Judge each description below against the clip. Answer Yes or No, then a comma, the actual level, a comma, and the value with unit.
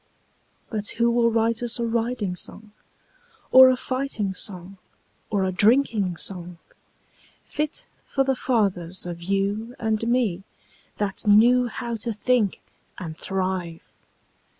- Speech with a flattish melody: No, average, 4.0 semitones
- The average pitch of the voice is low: No, high, 215 Hz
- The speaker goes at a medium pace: No, slow, 125 wpm